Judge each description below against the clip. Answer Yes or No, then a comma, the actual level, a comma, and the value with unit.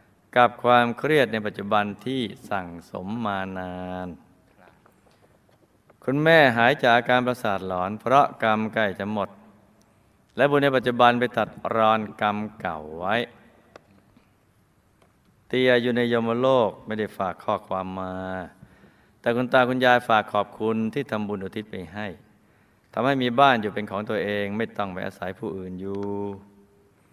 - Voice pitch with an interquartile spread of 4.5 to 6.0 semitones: No, average, 3.5 semitones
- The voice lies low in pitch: Yes, low, 105 Hz